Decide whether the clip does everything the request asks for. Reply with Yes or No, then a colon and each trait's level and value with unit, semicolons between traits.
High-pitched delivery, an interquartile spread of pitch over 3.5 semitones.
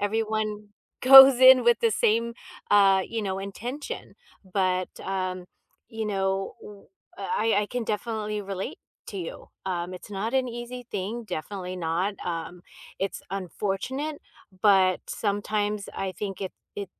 No: high, 205 Hz; average, 2.9 semitones